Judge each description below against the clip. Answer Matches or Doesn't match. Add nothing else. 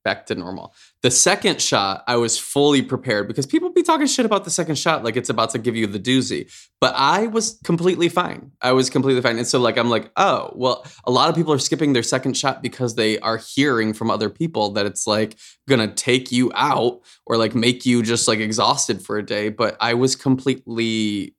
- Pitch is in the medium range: Doesn't match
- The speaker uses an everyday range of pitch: Matches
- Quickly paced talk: Matches